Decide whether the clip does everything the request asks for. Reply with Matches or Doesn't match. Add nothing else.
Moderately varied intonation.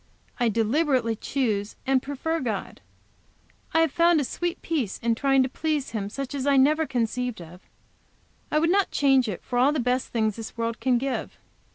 Matches